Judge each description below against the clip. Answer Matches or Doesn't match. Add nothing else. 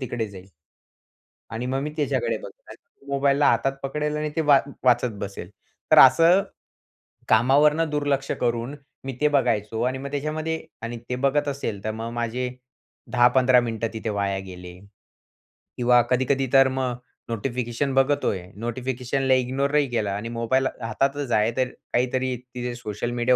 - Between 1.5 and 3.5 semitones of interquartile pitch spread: Matches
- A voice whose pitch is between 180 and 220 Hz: Doesn't match